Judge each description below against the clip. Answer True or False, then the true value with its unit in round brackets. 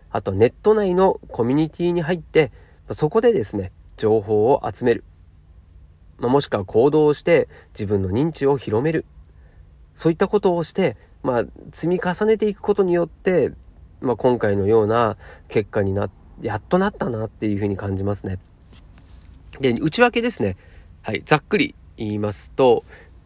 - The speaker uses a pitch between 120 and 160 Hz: False (110 Hz)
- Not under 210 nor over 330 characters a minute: True (315 characters per minute)